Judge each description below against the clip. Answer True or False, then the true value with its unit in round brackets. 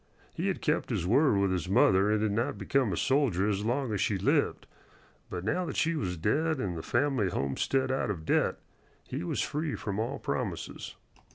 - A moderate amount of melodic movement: False (6.2 semitones)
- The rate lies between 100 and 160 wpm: False (200 wpm)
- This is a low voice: True (105 Hz)